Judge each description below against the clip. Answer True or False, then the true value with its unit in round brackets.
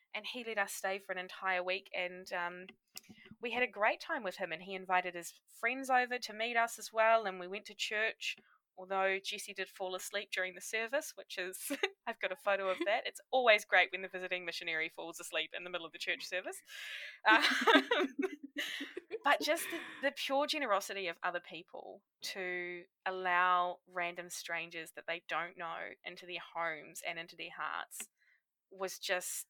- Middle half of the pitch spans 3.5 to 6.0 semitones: True (4.3 semitones)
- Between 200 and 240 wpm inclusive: False (190 wpm)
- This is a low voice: False (190 Hz)